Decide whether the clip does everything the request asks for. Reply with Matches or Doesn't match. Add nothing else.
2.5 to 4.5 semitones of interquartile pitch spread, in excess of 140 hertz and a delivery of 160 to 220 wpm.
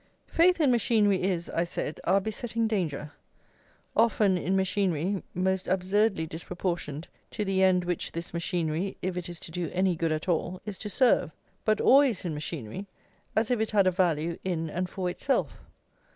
Matches